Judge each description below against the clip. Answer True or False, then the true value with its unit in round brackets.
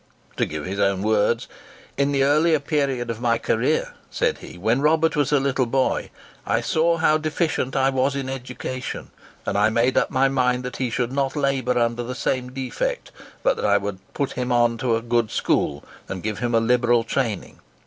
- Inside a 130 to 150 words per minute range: False (195 wpm)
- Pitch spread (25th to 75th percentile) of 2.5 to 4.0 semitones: True (3.1 semitones)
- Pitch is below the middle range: True (125 Hz)